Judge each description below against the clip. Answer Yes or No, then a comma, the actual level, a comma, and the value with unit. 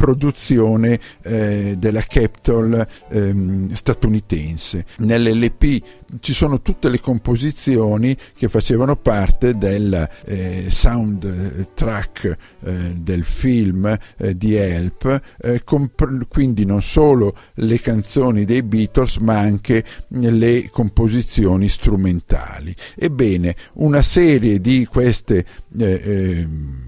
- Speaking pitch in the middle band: No, low, 110 Hz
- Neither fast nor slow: No, slow, 105 wpm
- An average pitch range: Yes, average, 4.2 semitones